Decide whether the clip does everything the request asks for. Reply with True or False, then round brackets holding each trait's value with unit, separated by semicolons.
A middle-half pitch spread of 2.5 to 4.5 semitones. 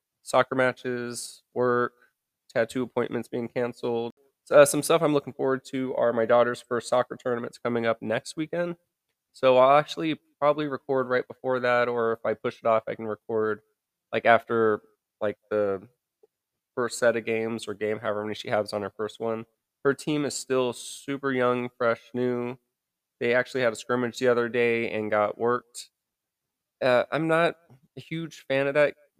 True (2.8 semitones)